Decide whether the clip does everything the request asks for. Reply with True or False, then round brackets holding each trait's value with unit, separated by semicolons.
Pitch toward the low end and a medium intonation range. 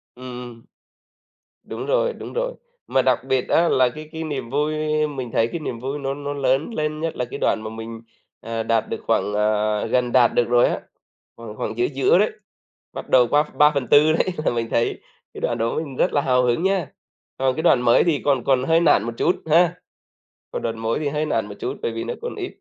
True (130 Hz; 4.8 semitones)